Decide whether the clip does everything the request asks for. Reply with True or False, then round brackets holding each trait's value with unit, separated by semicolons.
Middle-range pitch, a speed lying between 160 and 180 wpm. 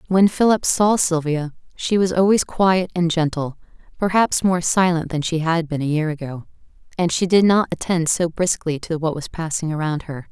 False (170 Hz; 190 wpm)